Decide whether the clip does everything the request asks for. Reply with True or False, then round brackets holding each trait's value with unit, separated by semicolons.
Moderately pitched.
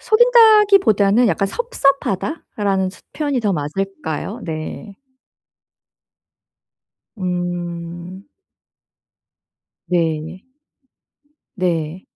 False (195 Hz)